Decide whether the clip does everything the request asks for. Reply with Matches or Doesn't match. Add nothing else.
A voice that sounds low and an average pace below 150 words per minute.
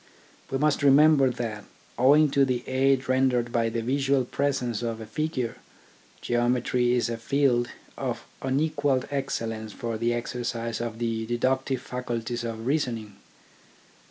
Matches